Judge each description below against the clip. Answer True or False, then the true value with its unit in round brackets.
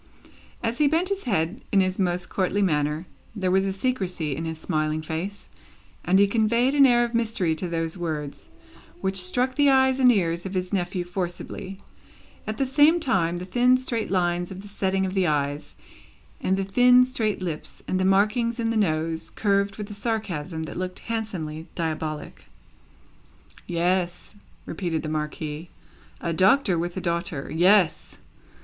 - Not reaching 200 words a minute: True (170 wpm)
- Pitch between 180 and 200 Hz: True (190 Hz)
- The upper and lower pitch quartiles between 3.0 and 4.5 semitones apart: False (5.0 semitones)